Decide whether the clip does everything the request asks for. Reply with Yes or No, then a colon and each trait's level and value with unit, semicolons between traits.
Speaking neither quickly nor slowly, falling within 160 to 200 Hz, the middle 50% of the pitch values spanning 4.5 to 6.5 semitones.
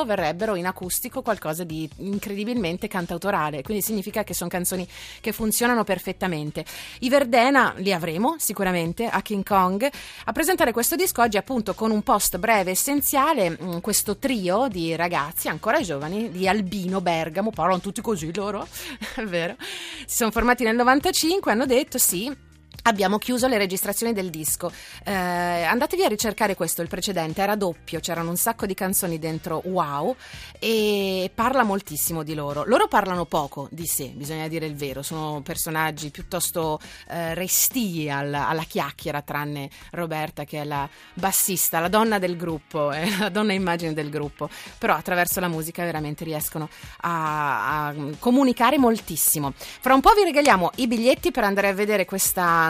Yes: average, 160 wpm; medium, 185 Hz; average, 5.3 semitones